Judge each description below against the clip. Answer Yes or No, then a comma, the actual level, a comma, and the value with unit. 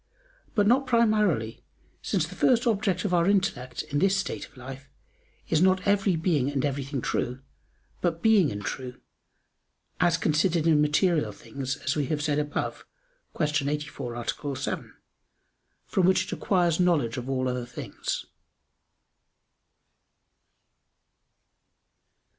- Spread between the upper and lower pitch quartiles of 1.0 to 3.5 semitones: No, wide, 5.6 semitones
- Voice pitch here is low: No, medium, 155 Hz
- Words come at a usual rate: No, slow, 130 wpm